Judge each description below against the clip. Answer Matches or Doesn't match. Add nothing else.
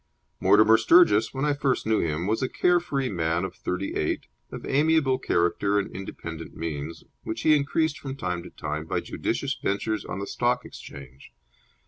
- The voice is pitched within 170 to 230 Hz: Doesn't match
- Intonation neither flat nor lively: Doesn't match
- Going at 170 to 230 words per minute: Matches